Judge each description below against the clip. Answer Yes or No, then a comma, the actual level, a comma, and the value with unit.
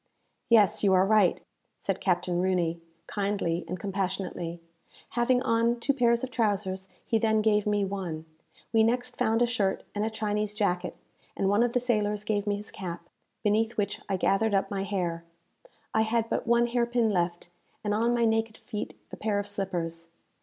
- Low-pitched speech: No, high, 205 Hz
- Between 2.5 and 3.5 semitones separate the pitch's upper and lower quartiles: Yes, average, 3.2 semitones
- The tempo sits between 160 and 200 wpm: Yes, average, 180 wpm